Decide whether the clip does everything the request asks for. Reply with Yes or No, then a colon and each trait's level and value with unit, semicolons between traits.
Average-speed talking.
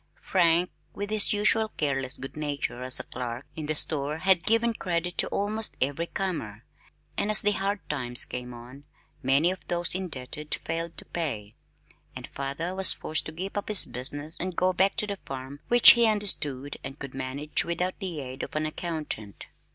Yes: average, 180 wpm